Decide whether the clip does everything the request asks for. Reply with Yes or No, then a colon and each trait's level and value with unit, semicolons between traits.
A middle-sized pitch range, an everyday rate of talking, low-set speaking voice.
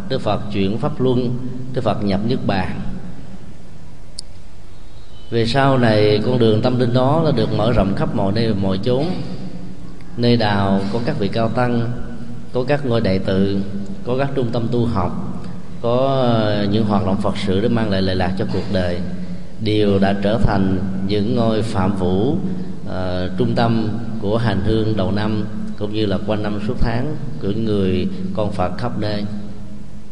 Yes: average, 3.4 semitones; average, 175 wpm; low, 105 Hz